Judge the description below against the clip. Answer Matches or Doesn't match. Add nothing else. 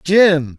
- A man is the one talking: Matches